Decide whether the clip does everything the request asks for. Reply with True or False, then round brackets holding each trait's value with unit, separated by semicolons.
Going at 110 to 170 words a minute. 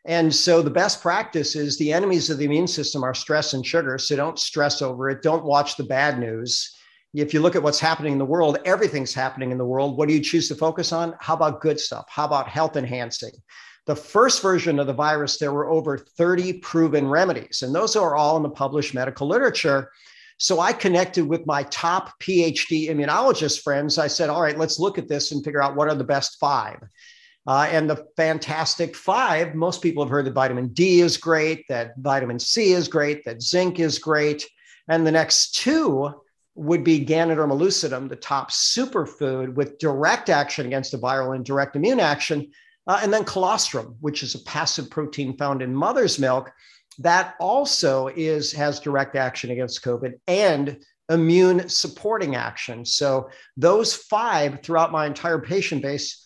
False (190 wpm)